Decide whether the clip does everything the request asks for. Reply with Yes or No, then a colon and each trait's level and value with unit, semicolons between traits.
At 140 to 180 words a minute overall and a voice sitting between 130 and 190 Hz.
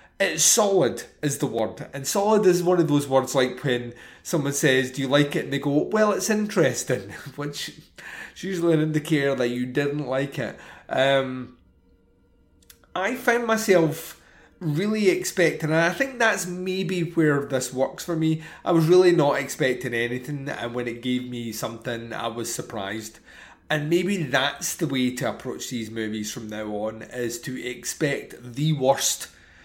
Yes: average, 170 wpm; medium, 140 Hz